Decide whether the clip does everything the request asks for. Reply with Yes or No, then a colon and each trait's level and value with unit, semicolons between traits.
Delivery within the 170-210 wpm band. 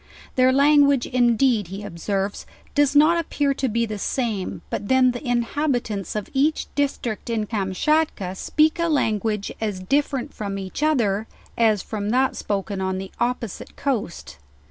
No: average, 150 wpm